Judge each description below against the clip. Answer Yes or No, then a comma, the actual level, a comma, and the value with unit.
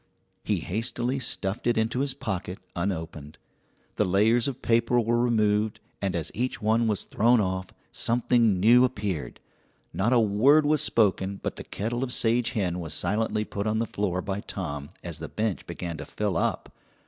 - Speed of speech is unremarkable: Yes, average, 175 wpm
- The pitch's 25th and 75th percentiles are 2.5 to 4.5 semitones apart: Yes, average, 4.1 semitones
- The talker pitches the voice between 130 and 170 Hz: No, low, 105 Hz